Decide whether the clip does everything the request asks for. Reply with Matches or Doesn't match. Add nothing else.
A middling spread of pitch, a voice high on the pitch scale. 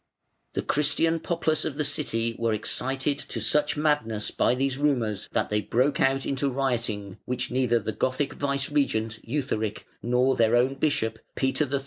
Doesn't match